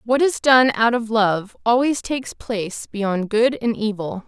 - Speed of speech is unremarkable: Yes, average, 180 wpm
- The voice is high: Yes, high, 225 Hz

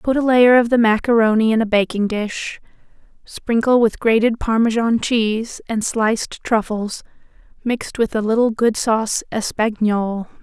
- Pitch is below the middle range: No, high, 225 Hz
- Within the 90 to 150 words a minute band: Yes, average, 145 wpm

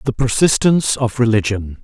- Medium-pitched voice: No, low, 120 Hz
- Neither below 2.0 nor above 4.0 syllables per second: No, 5.4 syllables/s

